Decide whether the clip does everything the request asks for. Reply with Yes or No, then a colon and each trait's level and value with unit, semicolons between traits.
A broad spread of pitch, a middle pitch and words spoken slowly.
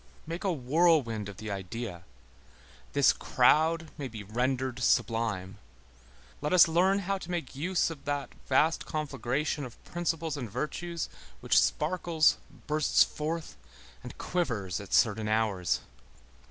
Yes: wide, 6.6 semitones; medium, 145 Hz; slow, 130 wpm